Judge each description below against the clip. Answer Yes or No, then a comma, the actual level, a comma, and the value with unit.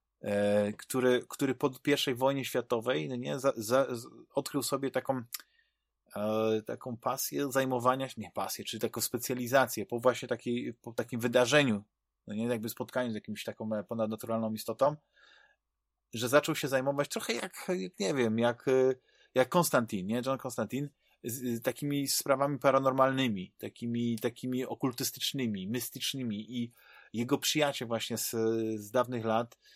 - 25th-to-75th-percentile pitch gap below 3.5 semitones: Yes, average, 2.9 semitones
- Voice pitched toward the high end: No, low, 125 Hz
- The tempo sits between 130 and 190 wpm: Yes, average, 145 wpm